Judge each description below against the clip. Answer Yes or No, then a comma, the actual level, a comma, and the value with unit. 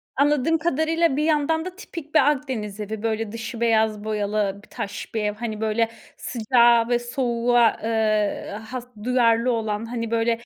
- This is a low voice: No, high, 230 Hz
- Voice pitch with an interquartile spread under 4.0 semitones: Yes, average, 3.2 semitones